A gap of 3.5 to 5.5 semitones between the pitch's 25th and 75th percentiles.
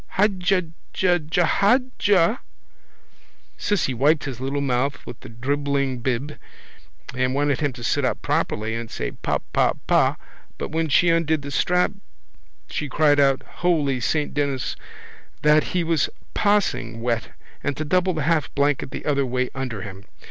Yes: average, 4.4 semitones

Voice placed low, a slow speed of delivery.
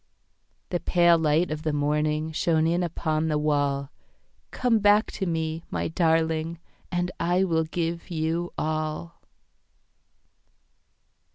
No: medium, 160 Hz; slow, 105 wpm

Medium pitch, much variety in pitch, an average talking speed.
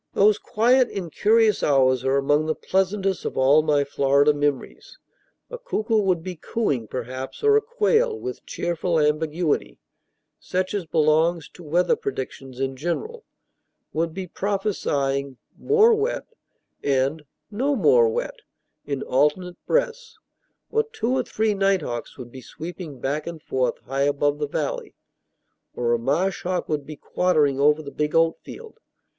Yes: medium, 165 Hz; wide, 7.1 semitones; average, 150 wpm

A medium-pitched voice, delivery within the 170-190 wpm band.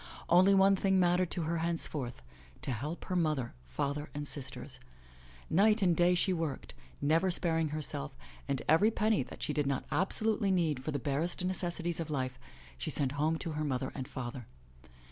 Yes: medium, 160 Hz; average, 180 wpm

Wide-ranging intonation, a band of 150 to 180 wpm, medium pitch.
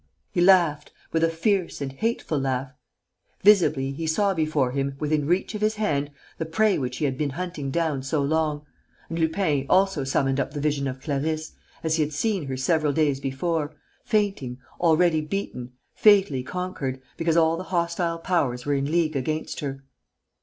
No: average, 3.9 semitones; average, 175 wpm; medium, 155 Hz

